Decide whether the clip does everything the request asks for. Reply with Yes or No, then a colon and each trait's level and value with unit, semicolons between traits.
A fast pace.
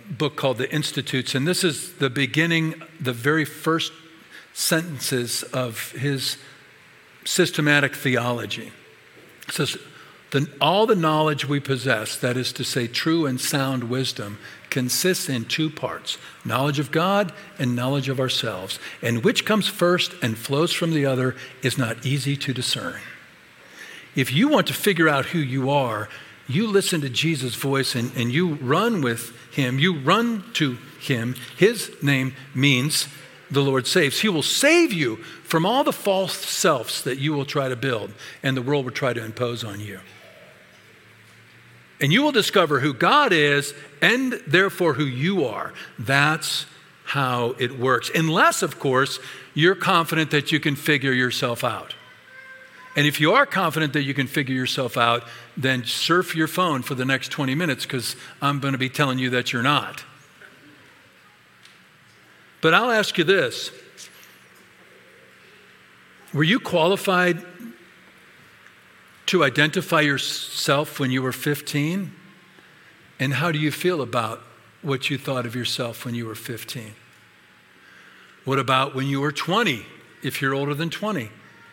No: average, 155 wpm